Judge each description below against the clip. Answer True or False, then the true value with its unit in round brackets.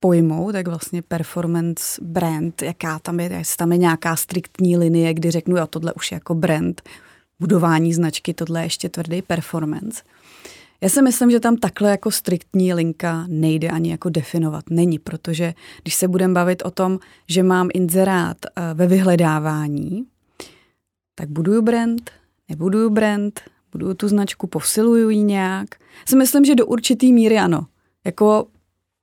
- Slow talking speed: False (155 wpm)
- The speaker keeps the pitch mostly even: False (3.0 semitones)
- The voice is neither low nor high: True (175 Hz)